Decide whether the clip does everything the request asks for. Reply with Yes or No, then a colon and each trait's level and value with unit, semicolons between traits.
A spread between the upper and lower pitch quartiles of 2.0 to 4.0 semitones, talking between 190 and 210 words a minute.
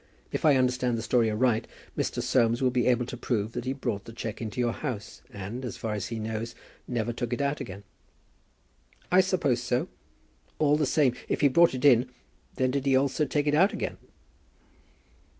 Yes: average, 3.1 semitones; average, 200 wpm